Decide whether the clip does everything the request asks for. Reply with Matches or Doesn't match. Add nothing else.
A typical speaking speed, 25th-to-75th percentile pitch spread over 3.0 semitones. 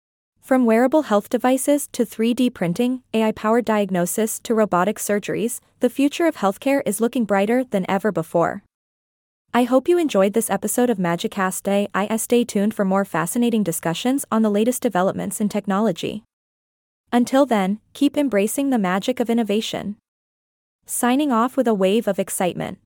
Matches